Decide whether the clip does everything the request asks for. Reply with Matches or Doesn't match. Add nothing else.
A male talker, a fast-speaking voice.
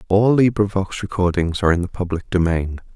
Doesn't match